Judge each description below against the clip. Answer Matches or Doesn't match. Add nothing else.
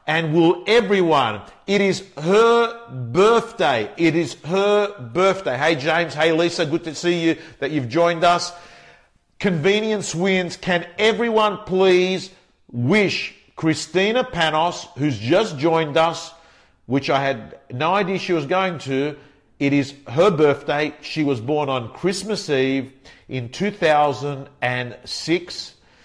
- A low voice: Doesn't match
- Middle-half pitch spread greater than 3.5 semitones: Matches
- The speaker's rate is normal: Doesn't match